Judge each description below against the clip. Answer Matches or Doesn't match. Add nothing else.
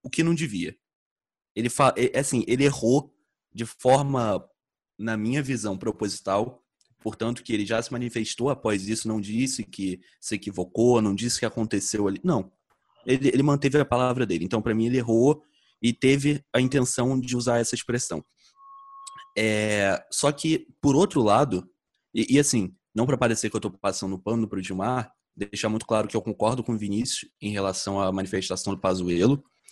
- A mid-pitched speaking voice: Doesn't match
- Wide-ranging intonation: Doesn't match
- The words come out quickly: Doesn't match